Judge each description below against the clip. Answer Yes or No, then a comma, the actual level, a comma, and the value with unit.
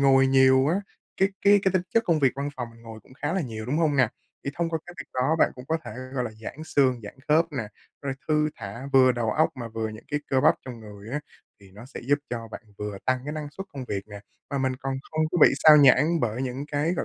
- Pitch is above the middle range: No, low, 135 Hz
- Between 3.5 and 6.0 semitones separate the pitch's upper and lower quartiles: Yes, average, 4.5 semitones